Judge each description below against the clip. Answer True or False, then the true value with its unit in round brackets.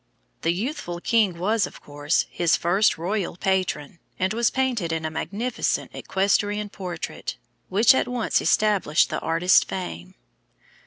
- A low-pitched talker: False (190 Hz)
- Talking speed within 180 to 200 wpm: False (140 wpm)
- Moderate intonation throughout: True (4.2 semitones)